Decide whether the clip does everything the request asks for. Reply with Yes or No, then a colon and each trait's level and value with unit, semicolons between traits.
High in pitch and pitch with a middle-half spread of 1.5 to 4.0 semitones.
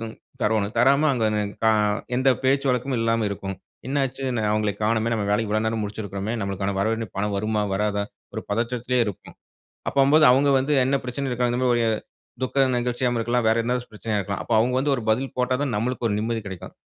No: low, 115 Hz; average, 3.2 semitones